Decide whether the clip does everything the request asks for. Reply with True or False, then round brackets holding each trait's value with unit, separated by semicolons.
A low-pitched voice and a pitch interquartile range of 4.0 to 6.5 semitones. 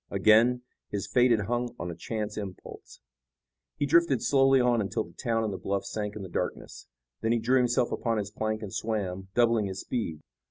False (110 Hz; 3.4 semitones)